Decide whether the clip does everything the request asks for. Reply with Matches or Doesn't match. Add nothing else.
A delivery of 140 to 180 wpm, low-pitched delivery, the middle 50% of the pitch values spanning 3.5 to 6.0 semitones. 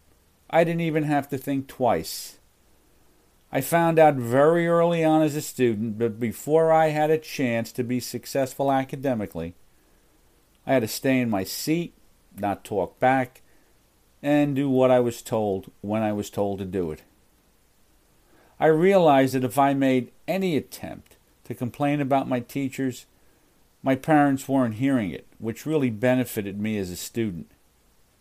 Matches